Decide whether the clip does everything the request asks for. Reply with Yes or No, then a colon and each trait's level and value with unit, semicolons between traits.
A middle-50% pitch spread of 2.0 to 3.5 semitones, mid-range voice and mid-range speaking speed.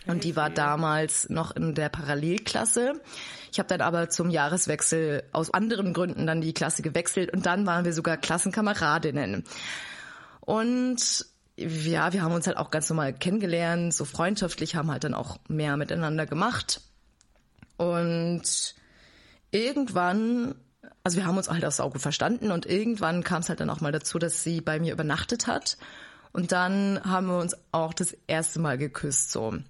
Yes: average, 2.8 semitones; medium, 170 Hz; average, 170 wpm